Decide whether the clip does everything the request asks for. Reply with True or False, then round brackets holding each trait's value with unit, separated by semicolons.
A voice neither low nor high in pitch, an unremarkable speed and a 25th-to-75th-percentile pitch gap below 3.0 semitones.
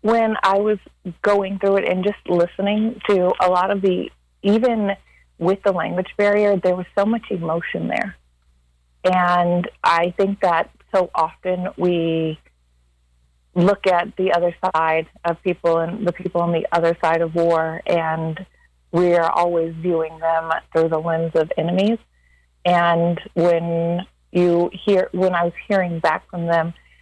True (175 Hz; 155 wpm; 2.6 semitones)